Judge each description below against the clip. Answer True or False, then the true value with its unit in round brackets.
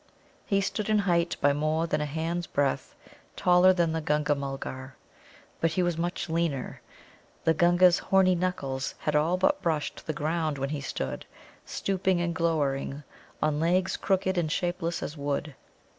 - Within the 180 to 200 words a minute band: False (160 wpm)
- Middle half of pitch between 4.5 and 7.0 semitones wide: False (3.2 semitones)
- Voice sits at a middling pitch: True (165 Hz)